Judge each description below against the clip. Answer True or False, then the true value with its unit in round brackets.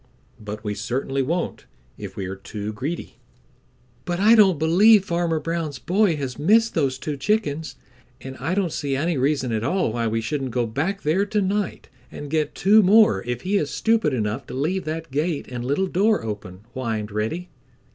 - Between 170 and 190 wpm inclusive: True (185 wpm)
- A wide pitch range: True (7.2 semitones)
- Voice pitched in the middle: True (150 Hz)